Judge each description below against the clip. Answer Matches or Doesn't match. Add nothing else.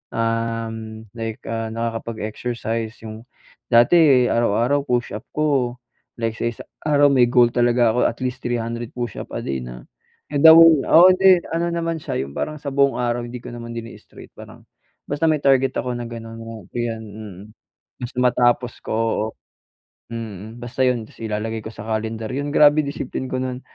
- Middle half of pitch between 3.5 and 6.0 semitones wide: Doesn't match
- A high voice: Doesn't match